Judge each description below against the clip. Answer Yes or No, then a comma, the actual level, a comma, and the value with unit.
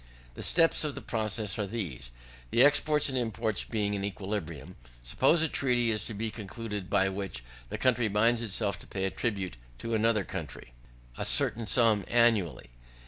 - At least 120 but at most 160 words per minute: No, average, 170 wpm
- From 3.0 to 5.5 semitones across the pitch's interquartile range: Yes, average, 3.3 semitones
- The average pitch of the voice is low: Yes, low, 110 Hz